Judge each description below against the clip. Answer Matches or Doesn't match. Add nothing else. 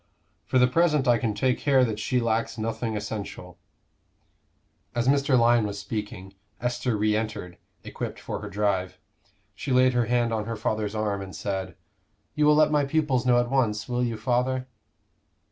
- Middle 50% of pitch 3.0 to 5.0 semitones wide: Matches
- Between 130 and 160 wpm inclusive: Doesn't match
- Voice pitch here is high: Doesn't match